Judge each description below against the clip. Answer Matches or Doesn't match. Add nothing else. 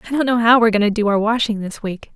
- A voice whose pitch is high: Matches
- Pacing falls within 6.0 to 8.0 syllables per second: Matches